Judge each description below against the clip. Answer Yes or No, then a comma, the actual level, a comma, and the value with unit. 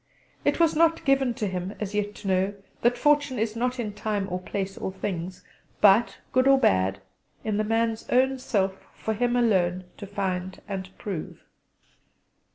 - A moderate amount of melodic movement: Yes, average, 4.4 semitones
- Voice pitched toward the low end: No, high, 210 Hz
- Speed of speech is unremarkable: Yes, average, 170 wpm